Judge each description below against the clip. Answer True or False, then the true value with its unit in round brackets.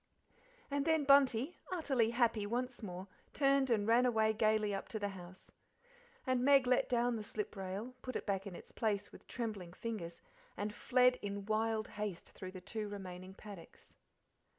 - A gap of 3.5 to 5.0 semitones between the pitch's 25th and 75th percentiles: True (3.9 semitones)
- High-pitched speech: True (220 Hz)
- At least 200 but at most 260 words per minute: False (175 wpm)